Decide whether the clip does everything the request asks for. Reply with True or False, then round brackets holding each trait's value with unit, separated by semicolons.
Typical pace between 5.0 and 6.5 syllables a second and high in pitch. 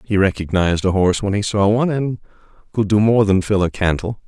False (6.1 syllables/s; 100 Hz)